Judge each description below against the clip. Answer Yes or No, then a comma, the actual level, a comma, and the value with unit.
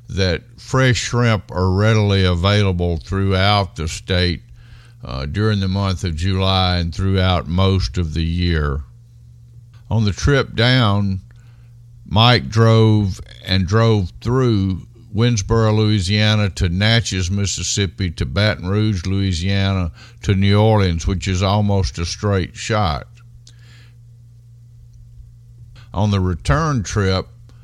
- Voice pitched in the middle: No, low, 105 Hz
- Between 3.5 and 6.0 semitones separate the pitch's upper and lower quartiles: Yes, average, 3.8 semitones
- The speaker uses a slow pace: Yes, slow, 115 wpm